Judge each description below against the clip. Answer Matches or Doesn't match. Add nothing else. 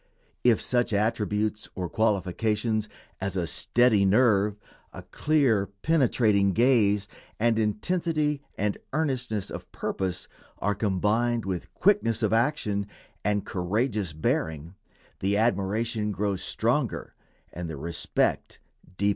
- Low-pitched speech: Matches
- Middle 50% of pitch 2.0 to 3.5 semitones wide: Matches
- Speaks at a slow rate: Matches